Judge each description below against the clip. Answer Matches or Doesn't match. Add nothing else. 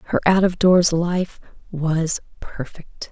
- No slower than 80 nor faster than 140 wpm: Matches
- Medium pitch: Matches